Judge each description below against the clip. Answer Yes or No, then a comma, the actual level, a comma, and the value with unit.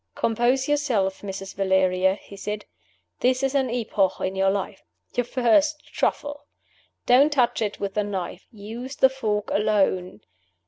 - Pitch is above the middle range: Yes, high, 215 Hz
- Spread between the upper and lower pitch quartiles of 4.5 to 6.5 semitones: Yes, average, 5.0 semitones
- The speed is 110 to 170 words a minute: Yes, average, 145 wpm